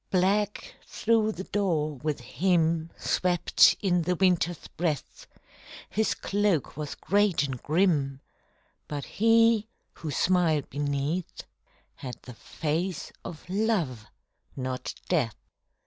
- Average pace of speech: No, slow, 115 wpm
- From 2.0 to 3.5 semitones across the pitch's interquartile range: No, average, 4.9 semitones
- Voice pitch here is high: No, medium, 170 Hz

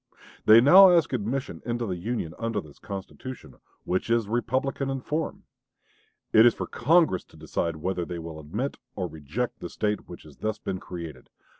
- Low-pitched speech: Yes, low, 110 Hz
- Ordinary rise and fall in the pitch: No, wide, 6.6 semitones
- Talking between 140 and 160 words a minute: No, average, 175 wpm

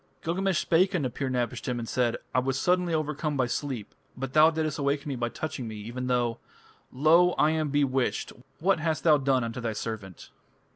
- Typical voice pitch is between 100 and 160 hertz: Yes, low, 135 Hz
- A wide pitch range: No, average, 4.3 semitones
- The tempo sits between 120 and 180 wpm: No, average, 190 wpm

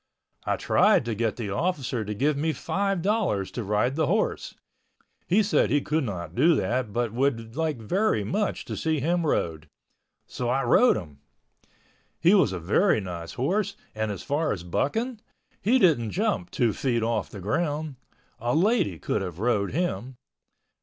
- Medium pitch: No, low, 130 Hz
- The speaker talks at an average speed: Yes, average, 175 wpm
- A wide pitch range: Yes, wide, 8.1 semitones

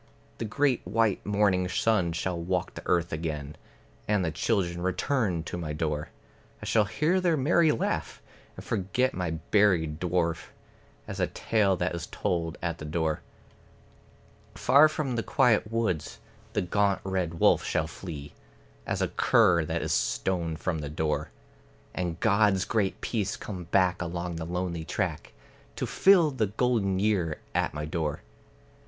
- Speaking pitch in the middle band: No, very low, 90 Hz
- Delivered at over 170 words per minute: No, average, 155 wpm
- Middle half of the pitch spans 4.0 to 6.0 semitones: Yes, average, 4.4 semitones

